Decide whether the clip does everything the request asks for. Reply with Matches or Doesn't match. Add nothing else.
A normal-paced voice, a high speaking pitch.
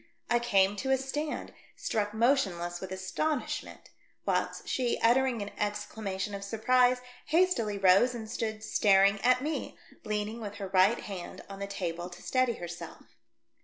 Matches